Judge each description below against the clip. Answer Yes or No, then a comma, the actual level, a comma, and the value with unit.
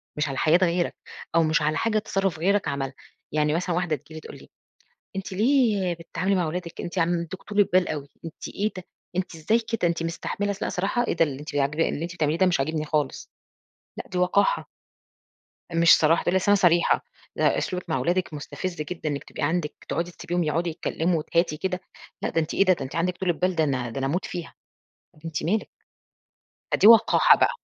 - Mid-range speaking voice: Yes, medium, 170 Hz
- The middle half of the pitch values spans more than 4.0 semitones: No, average, 3.2 semitones